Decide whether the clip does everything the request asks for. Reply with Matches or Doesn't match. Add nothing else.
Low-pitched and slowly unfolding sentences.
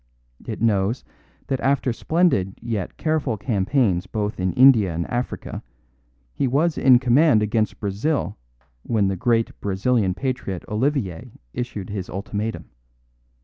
Matches